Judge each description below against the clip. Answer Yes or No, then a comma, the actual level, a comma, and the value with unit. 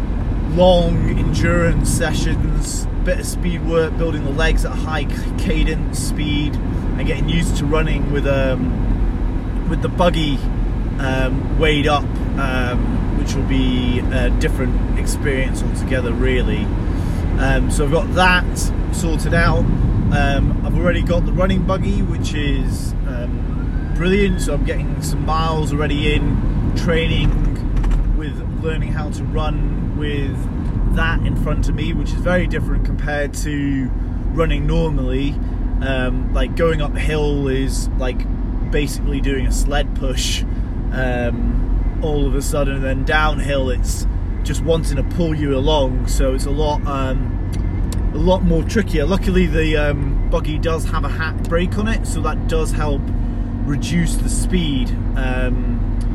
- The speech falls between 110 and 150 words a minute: Yes, average, 145 wpm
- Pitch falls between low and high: No, low, 110 Hz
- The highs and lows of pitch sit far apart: Yes, wide, 7.0 semitones